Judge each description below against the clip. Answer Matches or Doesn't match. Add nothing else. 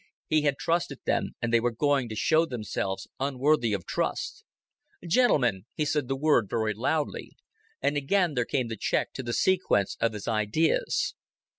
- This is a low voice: Matches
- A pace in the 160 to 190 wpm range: Matches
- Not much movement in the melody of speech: Doesn't match